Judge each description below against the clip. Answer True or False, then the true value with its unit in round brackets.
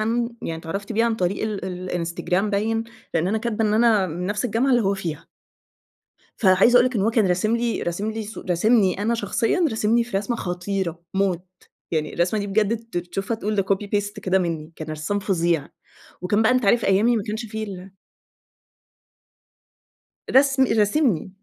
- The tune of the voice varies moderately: True (3.7 semitones)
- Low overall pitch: False (205 Hz)